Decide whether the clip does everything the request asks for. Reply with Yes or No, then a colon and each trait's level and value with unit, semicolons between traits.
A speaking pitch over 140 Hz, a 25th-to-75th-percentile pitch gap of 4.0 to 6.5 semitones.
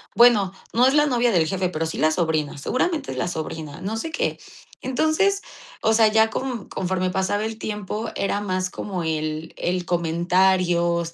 Yes: high, 190 Hz; average, 4.9 semitones